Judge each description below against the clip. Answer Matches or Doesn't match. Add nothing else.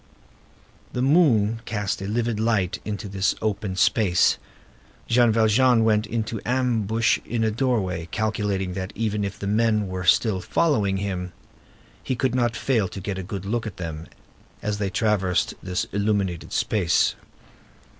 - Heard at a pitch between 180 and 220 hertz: Doesn't match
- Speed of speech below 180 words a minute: Matches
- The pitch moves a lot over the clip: Doesn't match